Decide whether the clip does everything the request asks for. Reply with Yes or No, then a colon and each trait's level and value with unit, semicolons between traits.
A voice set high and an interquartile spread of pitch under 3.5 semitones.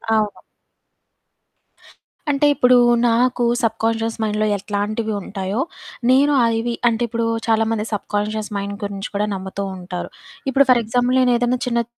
Yes: high, 225 Hz; average, 2.7 semitones